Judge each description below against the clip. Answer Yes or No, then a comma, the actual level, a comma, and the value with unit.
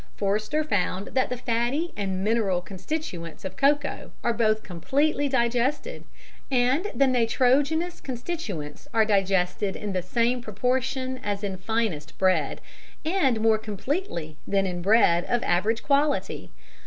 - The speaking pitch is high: Yes, high, 230 Hz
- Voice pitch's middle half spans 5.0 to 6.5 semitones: Yes, wide, 5.5 semitones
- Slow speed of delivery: Yes, slow, 130 wpm